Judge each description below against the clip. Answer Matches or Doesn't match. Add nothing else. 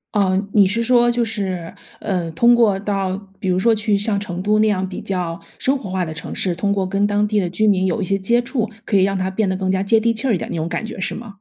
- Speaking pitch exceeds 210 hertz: Doesn't match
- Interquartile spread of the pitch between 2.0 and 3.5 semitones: Matches